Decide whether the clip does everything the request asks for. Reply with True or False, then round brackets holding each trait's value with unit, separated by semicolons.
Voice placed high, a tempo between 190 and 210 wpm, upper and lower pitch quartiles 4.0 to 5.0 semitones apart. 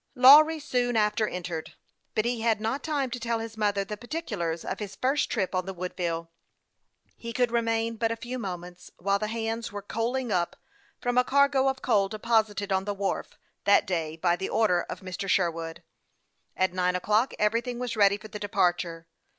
True (215 Hz; 200 wpm; 4.3 semitones)